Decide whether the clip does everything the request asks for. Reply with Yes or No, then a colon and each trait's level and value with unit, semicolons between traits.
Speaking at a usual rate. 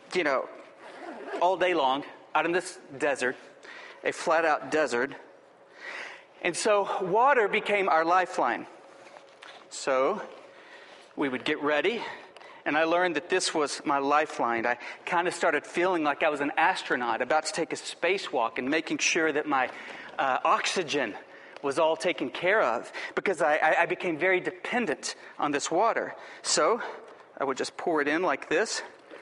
Yes: average, 160 wpm